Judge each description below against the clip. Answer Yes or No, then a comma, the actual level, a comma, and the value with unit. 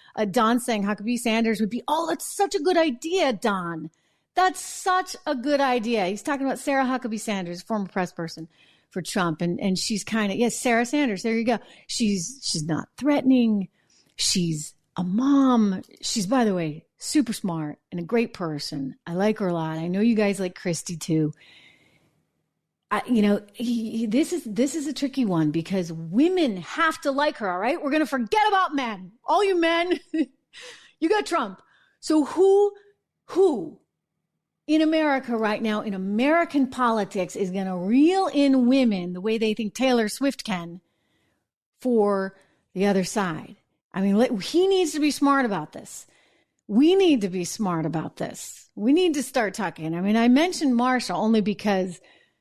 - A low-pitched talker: No, high, 230 Hz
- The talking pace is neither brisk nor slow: Yes, average, 180 wpm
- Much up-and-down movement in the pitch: Yes, wide, 7.0 semitones